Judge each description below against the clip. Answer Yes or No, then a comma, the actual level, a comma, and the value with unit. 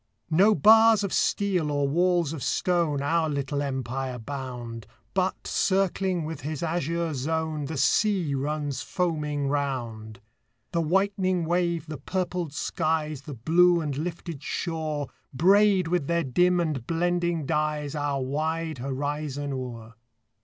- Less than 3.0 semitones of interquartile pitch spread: No, average, 3.8 semitones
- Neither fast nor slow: No, slow, 130 wpm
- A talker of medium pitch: Yes, medium, 155 Hz